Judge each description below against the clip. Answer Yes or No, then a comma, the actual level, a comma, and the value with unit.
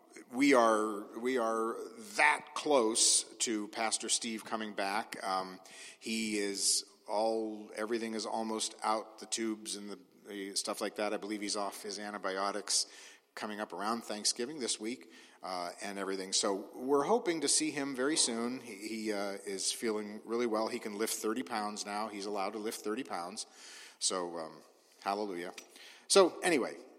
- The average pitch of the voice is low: Yes, low, 110 Hz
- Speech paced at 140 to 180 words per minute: Yes, average, 165 wpm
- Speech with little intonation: Yes, narrow, 2.1 semitones